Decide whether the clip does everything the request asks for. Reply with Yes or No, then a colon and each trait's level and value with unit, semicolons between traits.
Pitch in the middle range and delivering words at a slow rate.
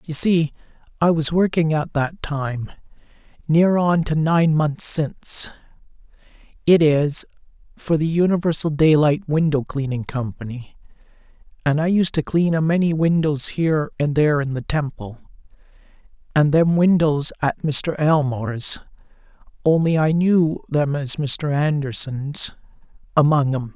Yes: medium, 150 Hz; slow, 120 wpm